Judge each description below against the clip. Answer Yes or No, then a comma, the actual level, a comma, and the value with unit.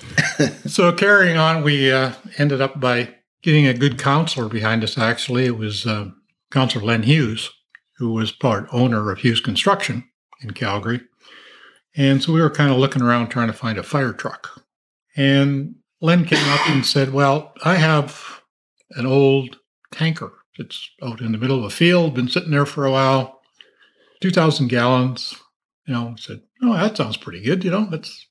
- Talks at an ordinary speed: Yes, average, 180 wpm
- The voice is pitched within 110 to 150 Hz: Yes, low, 135 Hz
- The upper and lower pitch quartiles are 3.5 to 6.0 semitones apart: Yes, average, 4.3 semitones